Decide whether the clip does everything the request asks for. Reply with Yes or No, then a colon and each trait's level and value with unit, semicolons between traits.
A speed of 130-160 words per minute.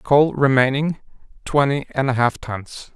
Yes: average, 140 wpm